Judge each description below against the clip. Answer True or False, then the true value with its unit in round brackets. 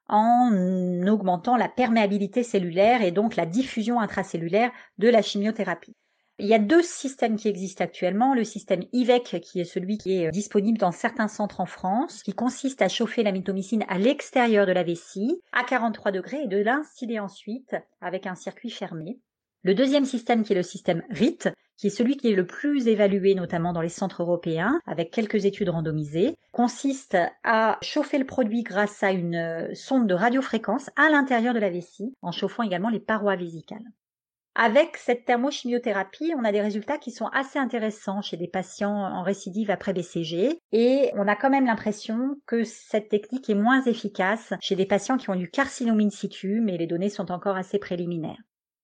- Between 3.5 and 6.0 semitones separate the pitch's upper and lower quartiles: True (4.2 semitones)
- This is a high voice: True (210 Hz)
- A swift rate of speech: False (185 wpm)